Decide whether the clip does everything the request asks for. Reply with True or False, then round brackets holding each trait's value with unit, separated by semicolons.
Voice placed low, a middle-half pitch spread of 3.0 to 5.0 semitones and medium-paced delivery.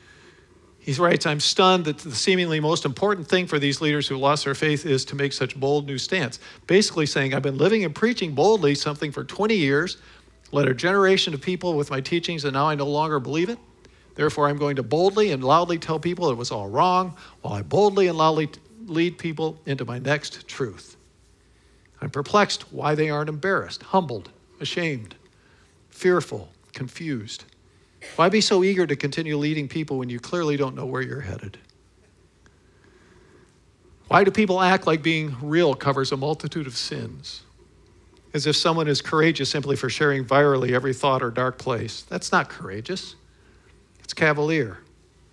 False (145 Hz; 4.2 semitones; 175 wpm)